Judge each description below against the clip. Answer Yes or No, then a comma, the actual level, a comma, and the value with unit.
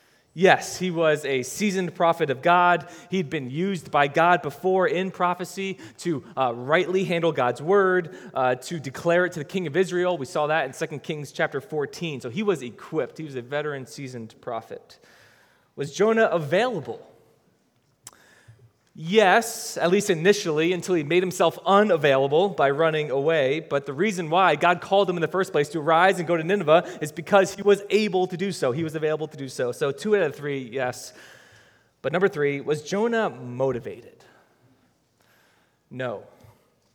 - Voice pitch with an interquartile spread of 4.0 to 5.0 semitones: Yes, average, 4.4 semitones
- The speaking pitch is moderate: Yes, medium, 170 Hz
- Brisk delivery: No, average, 175 wpm